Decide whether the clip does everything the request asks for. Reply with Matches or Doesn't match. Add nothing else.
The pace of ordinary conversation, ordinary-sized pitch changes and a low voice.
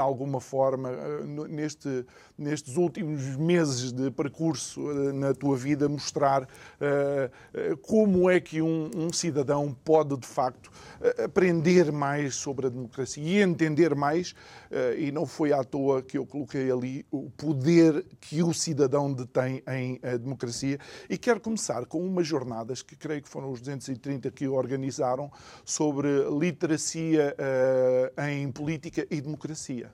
Doesn't match